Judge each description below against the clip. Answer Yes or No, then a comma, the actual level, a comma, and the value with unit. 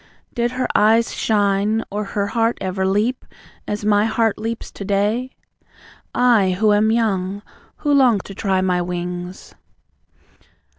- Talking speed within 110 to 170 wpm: Yes, average, 140 wpm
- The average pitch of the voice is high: Yes, high, 210 Hz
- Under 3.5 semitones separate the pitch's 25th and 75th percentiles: Yes, average, 2.8 semitones